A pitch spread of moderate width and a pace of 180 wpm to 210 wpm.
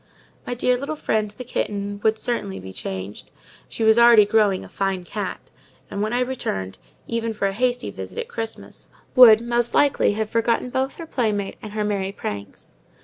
Yes: average, 3.3 semitones; average, 185 wpm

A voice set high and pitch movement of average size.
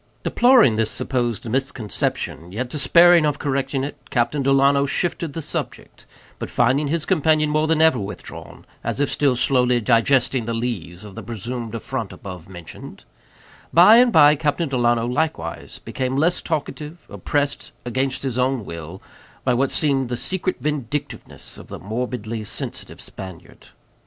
No: low, 130 Hz; average, 4.4 semitones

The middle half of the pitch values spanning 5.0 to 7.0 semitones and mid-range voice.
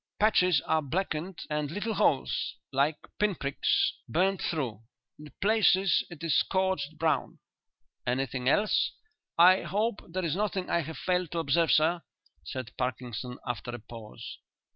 Yes: wide, 5.6 semitones; medium, 160 Hz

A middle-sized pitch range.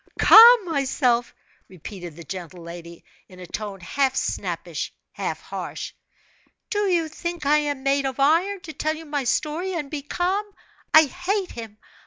No: wide, 8.0 semitones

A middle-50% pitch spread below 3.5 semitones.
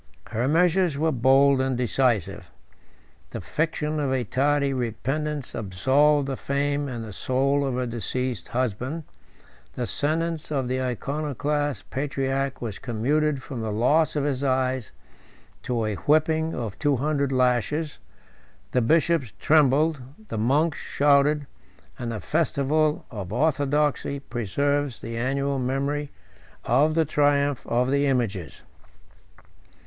Yes: average, 3.0 semitones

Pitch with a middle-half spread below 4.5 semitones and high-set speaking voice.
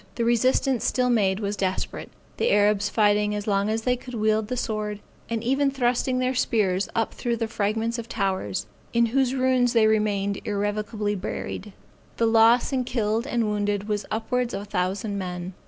Yes: average, 2.7 semitones; high, 220 Hz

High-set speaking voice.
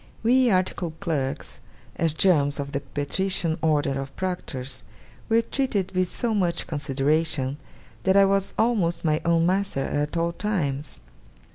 No: medium, 165 Hz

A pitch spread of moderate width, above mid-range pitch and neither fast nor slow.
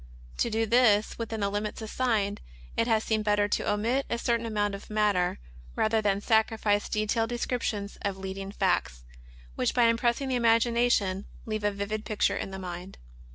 No: narrow, 2.3 semitones; high, 215 Hz; average, 170 wpm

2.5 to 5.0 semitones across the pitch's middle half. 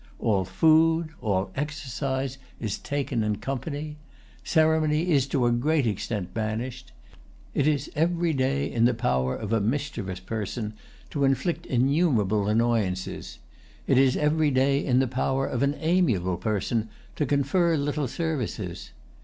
No: wide, 5.4 semitones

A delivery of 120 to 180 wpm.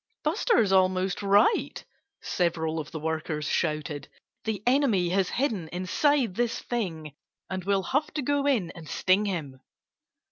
Yes: average, 140 wpm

